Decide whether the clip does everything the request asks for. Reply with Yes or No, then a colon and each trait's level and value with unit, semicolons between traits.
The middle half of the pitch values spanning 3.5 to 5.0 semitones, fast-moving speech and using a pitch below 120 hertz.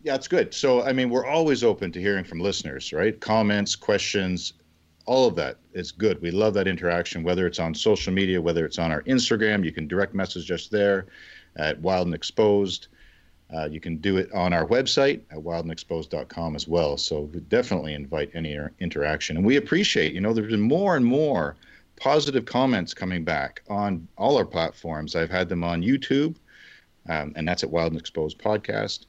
No: average, 3.9 semitones; average, 195 wpm; very low, 90 Hz